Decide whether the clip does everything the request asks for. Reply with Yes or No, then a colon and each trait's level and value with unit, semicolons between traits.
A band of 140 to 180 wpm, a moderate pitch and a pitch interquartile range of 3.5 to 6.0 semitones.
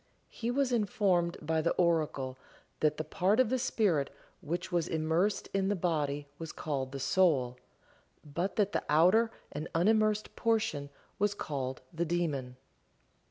Yes: average, 150 wpm; medium, 170 Hz; wide, 5.6 semitones